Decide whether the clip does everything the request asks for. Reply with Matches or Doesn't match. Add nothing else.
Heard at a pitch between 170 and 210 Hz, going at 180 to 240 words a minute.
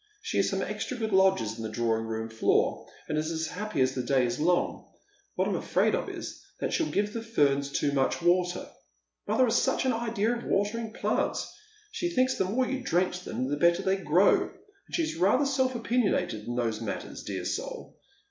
Matches